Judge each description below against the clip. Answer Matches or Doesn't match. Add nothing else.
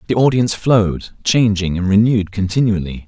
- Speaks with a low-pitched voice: Matches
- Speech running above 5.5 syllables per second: Matches